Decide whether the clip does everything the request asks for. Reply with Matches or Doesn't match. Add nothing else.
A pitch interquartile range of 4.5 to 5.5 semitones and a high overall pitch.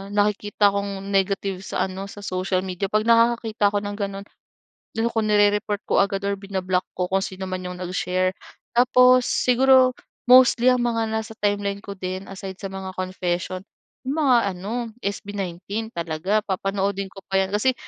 Doesn't match